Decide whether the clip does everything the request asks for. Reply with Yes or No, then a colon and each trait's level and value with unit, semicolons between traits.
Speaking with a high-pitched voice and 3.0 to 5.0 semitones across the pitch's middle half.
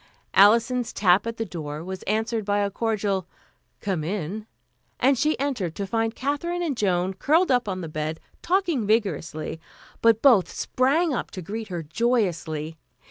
No: high, 210 Hz; wide, 5.6 semitones